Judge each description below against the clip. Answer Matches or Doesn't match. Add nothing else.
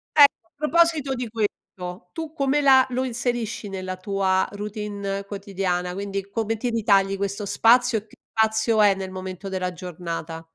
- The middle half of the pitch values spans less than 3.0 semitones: Doesn't match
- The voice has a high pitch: Matches